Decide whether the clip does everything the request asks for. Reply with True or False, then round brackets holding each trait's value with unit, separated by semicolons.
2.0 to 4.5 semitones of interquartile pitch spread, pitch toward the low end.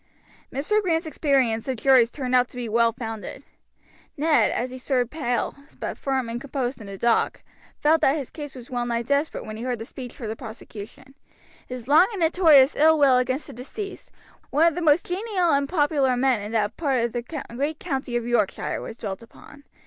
False (4.1 semitones; 260 Hz)